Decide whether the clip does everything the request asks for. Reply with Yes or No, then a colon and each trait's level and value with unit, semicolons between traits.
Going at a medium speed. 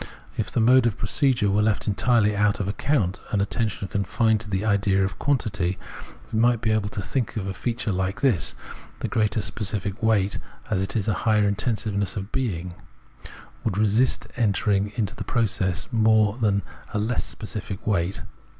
Yes: average, 180 wpm